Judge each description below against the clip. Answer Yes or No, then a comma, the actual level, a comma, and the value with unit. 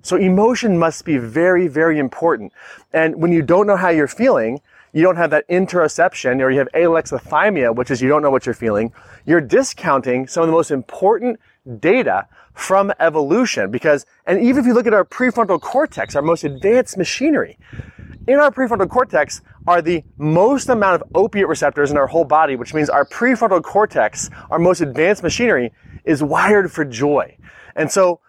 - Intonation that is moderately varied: No, wide, 5.9 semitones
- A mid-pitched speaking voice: Yes, medium, 165 Hz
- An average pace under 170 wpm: No, average, 180 wpm